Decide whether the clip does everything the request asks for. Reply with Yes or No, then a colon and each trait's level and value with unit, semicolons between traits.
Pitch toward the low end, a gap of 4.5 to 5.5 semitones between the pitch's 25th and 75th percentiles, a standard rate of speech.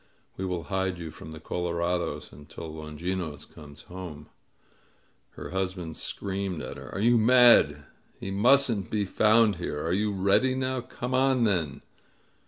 Yes: very low, 95 Hz; average, 5.0 semitones; average, 155 wpm